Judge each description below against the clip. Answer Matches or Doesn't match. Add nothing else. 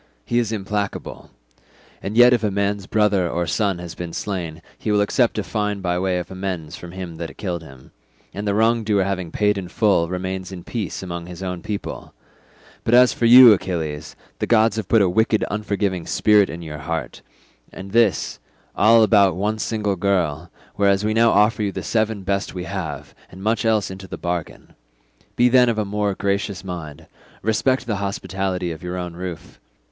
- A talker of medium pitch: Doesn't match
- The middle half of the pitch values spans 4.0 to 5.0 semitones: Doesn't match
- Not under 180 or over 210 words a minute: Matches